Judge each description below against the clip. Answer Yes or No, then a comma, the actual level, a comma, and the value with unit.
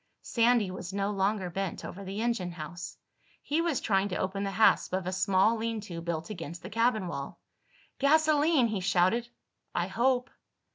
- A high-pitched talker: Yes, high, 200 Hz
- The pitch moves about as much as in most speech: Yes, average, 4.3 semitones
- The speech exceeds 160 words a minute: Yes, average, 175 wpm